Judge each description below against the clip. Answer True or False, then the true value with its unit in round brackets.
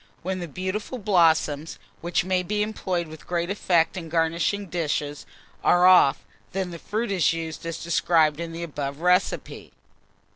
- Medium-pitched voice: True (170 Hz)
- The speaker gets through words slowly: False (155 wpm)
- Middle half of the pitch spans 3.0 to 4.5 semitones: False (2.4 semitones)